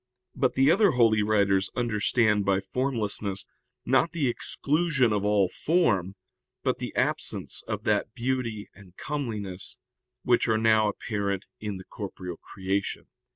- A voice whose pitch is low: Yes, low, 110 Hz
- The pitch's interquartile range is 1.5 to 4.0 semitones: No, average, 4.4 semitones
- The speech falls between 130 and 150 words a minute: Yes, slow, 135 wpm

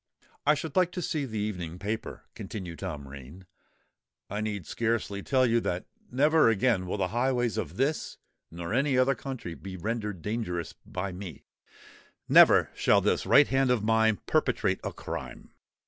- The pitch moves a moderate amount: No, wide, 5.8 semitones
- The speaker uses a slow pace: No, average, 160 wpm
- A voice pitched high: No, low, 110 Hz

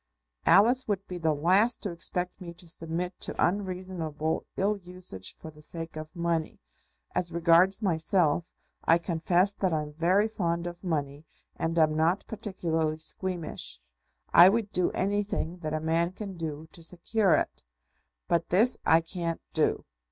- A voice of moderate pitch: Yes, medium, 170 Hz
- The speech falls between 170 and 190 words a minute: No, average, 155 wpm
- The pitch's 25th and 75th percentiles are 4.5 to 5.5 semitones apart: No, average, 2.7 semitones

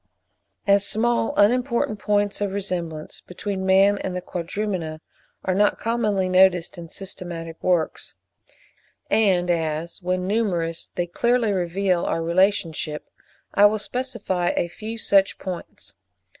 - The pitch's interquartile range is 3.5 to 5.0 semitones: No, average, 3.0 semitones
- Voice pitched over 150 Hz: Yes, high, 190 Hz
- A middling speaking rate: No, slow, 125 wpm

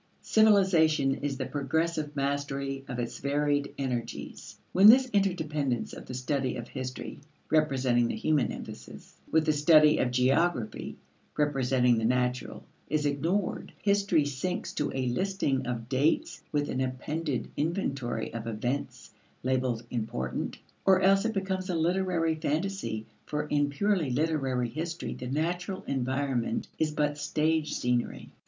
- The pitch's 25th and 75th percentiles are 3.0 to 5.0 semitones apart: Yes, average, 4.3 semitones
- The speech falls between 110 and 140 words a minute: Yes, slow, 135 wpm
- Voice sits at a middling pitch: Yes, medium, 145 Hz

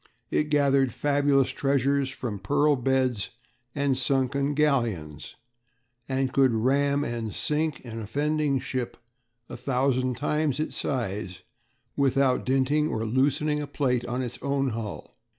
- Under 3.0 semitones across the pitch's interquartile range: Yes, narrow, 2.5 semitones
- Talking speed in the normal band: No, slow, 130 wpm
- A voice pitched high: No, low, 135 Hz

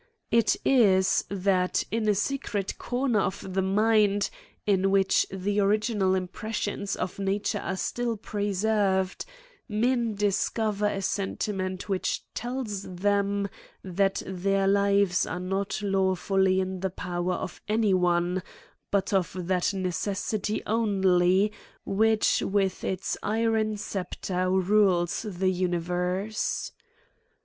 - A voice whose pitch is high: Yes, high, 195 Hz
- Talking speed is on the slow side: Yes, slow, 120 wpm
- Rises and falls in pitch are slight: Yes, narrow, 2.0 semitones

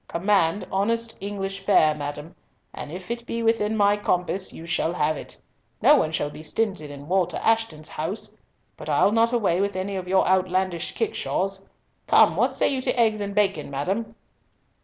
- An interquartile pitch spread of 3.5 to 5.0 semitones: Yes, average, 4.1 semitones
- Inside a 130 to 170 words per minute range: No, average, 180 wpm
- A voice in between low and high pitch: No, high, 195 Hz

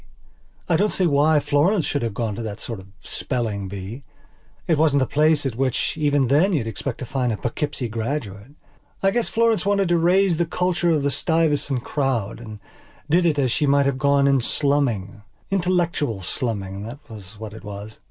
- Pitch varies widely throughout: Yes, wide, 6.1 semitones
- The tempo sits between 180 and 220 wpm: Yes, average, 190 wpm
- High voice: No, medium, 140 Hz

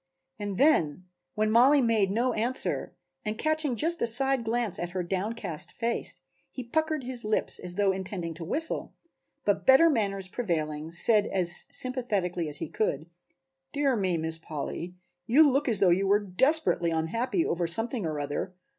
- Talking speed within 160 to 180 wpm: Yes, average, 165 wpm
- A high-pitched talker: Yes, high, 210 Hz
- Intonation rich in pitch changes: Yes, wide, 6.3 semitones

